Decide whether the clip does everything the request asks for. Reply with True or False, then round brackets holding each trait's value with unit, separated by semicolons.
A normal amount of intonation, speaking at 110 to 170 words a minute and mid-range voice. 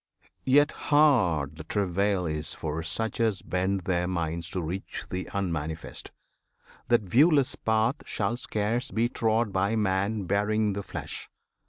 False (4.2 semitones; 140 wpm; 100 Hz)